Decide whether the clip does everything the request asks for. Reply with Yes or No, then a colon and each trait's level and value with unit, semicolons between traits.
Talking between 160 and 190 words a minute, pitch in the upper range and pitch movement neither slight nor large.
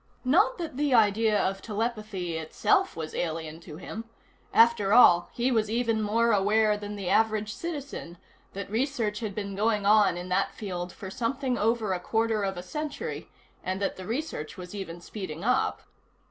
Yes: average, 175 wpm; high, 210 Hz; average, 3.6 semitones